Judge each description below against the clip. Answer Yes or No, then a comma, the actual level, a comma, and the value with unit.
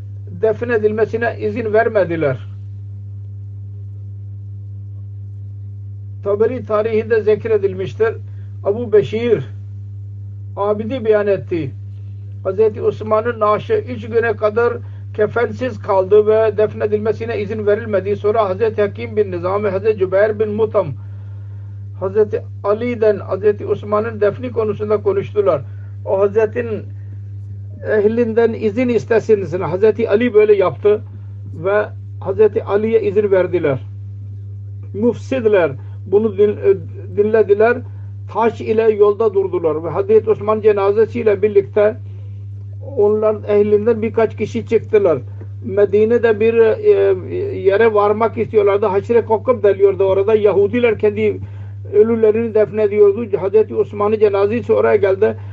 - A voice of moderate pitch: No, high, 205 Hz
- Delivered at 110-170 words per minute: No, average, 100 wpm